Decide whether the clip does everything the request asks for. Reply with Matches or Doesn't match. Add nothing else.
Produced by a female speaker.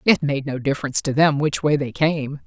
Matches